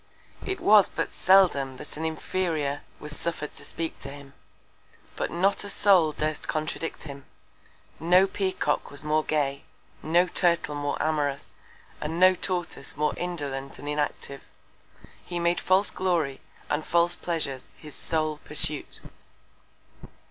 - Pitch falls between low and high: Yes, medium, 155 Hz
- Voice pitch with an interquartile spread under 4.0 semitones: Yes, average, 3.2 semitones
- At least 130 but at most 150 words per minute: Yes, slow, 135 wpm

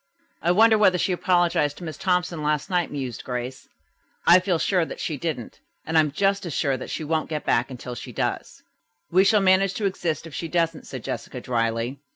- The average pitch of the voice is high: No, medium, 160 Hz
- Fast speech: Yes, fast, 210 wpm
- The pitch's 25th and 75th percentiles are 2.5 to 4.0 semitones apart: No, average, 4.9 semitones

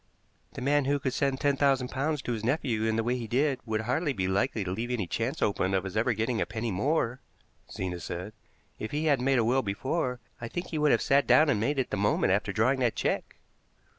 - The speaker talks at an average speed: No, fast, 245 wpm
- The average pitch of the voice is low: Yes, low, 125 Hz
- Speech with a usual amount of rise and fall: Yes, average, 4.1 semitones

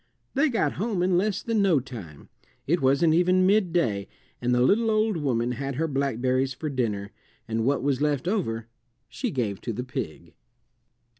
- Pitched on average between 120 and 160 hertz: Yes, medium, 140 Hz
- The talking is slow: No, average, 170 wpm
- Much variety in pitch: Yes, wide, 7.1 semitones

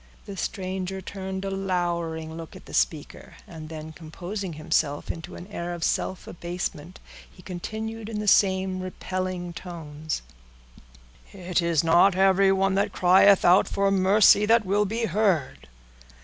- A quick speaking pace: No, average, 145 wpm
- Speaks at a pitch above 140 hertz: Yes, medium, 185 Hz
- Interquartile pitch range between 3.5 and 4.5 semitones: No, narrow, 2.4 semitones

